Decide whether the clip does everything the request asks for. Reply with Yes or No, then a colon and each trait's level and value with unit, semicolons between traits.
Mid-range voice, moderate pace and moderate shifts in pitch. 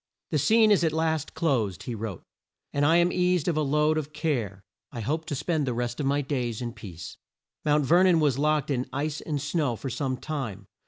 No: medium, 145 Hz; fast, 220 wpm; average, 4.4 semitones